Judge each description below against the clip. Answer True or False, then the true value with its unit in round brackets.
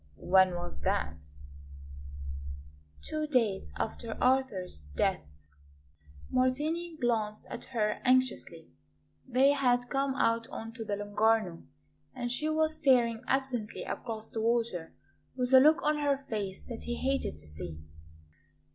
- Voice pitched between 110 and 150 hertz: False (240 Hz)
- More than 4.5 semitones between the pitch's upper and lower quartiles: False (4.1 semitones)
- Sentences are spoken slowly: True (130 wpm)